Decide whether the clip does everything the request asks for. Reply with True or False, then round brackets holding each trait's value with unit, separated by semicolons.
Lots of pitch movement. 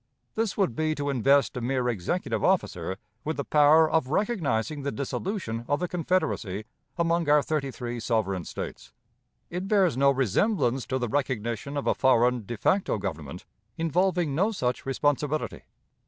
True (5.7 semitones)